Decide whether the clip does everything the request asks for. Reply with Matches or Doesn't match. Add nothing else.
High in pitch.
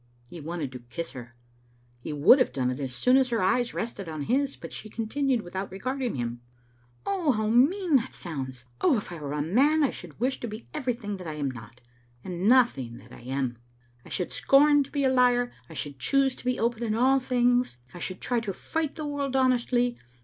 Matches